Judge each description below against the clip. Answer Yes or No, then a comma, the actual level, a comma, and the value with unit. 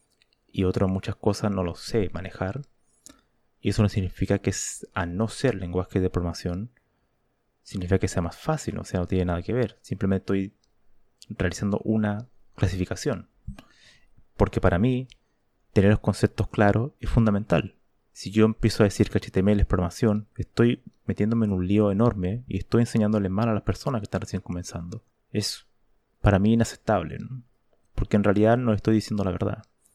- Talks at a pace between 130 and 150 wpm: No, average, 170 wpm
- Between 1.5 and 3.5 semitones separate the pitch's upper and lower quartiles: Yes, average, 2.9 semitones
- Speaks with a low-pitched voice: Yes, low, 105 Hz